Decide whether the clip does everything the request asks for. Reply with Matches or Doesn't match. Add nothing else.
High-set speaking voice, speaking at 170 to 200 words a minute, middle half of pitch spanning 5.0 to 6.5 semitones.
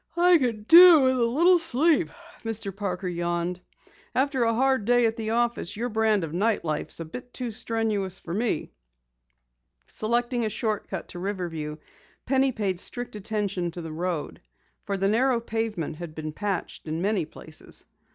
Matches